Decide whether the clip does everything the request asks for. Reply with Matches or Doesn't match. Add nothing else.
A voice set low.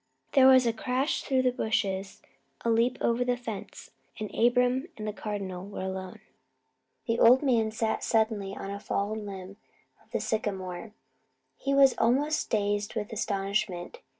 Doesn't match